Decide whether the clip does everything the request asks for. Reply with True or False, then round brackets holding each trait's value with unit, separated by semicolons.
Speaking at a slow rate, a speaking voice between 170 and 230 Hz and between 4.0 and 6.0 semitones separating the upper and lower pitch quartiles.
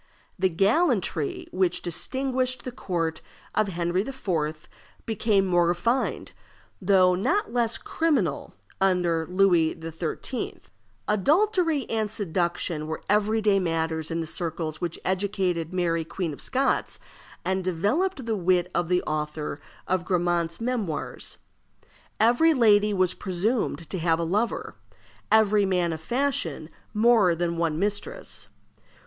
True (125 wpm; 185 Hz; 4.7 semitones)